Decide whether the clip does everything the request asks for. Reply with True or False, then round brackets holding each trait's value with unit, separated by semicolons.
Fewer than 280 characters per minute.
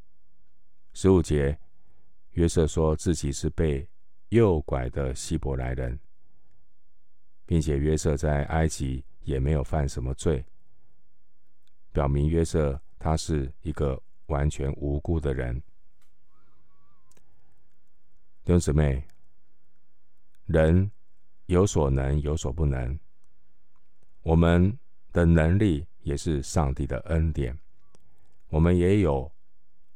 True (145 characters per minute)